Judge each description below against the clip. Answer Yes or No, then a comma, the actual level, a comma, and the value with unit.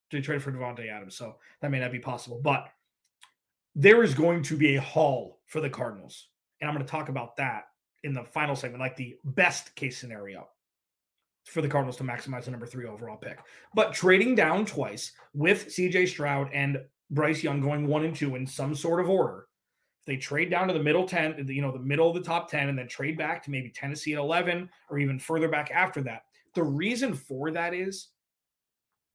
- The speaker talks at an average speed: No, fast, 210 wpm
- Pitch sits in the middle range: Yes, medium, 145 Hz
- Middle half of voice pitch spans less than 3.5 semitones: No, average, 3.8 semitones